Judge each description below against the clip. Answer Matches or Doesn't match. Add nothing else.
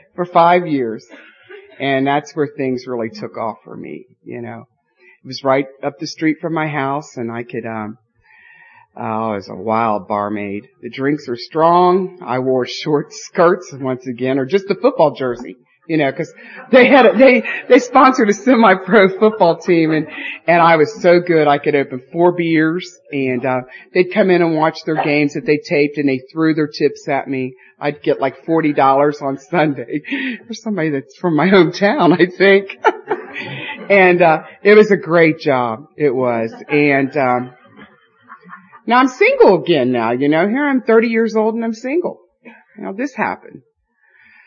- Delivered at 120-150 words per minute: Doesn't match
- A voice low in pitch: Doesn't match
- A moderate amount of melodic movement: Doesn't match